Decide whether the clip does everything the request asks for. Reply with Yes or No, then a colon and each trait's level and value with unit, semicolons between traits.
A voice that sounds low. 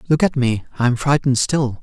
Yes: low, 130 Hz